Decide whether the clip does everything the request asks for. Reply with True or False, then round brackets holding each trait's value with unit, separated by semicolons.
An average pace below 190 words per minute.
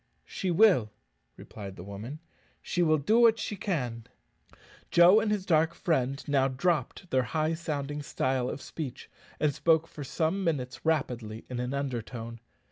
True (155 wpm)